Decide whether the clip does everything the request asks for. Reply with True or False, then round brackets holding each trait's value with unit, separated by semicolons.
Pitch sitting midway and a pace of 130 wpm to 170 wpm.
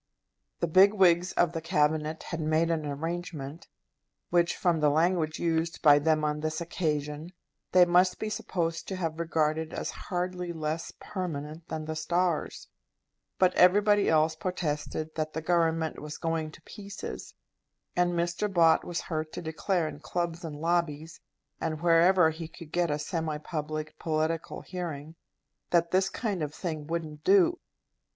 True (165 Hz; 155 wpm)